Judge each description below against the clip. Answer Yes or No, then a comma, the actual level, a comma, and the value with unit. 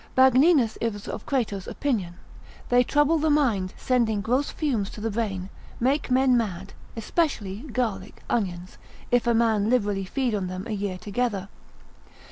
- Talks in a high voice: Yes, high, 225 Hz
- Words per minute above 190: No, average, 150 wpm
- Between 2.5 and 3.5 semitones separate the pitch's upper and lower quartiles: No, average, 4.3 semitones